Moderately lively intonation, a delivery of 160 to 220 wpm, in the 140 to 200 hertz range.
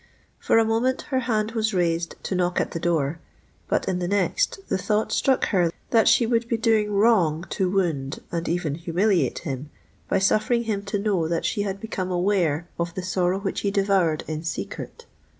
Yes: average, 4.2 semitones; average, 195 wpm; high, 190 Hz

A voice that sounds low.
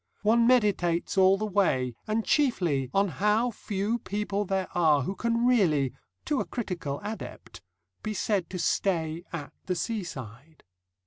No: high, 195 Hz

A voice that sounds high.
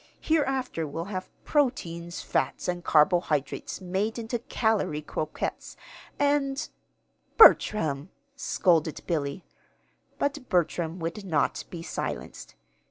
No: medium, 180 Hz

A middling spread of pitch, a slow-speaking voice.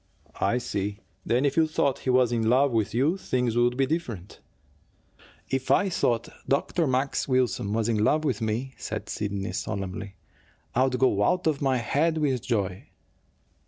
No: average, 4.0 semitones; average, 165 wpm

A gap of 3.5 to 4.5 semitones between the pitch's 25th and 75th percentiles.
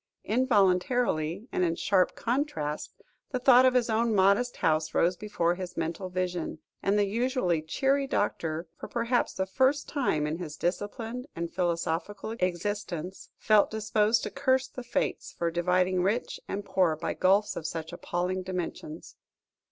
No: average, 5.1 semitones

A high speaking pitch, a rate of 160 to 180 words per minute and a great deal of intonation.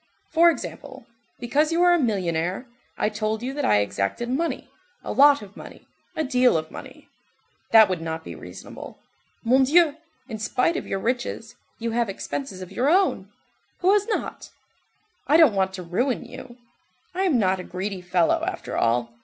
Yes: high, 240 Hz; average, 175 wpm; wide, 7.5 semitones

